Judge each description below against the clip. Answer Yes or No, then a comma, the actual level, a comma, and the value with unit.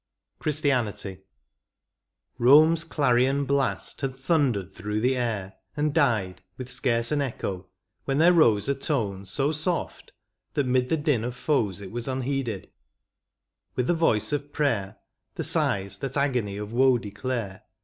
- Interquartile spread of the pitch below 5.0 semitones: No, average, 5.3 semitones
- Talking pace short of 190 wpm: Yes, average, 150 wpm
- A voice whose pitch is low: Yes, low, 125 Hz